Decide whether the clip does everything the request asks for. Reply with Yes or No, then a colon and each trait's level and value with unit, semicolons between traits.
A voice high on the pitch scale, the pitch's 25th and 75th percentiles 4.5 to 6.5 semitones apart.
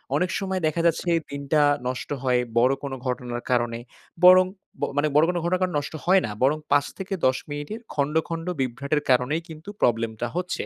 No: medium, 145 Hz; average, 5.3 semitones